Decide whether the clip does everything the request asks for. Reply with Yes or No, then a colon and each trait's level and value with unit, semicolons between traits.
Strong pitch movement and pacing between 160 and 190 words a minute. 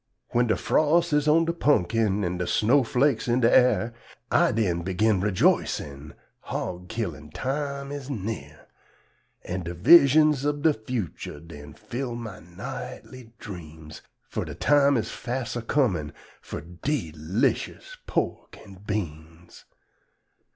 No: wide, 7.8 semitones; slow, 135 wpm